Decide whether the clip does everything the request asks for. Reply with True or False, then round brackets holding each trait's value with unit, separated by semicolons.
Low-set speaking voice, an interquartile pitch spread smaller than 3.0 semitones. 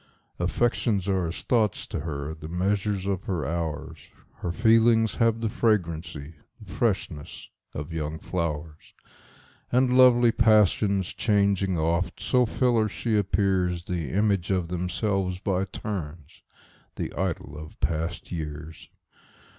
False (95 Hz; 4.6 semitones)